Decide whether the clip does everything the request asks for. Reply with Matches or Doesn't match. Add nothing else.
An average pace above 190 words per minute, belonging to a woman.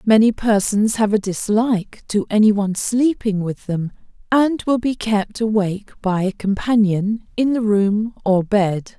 Doesn't match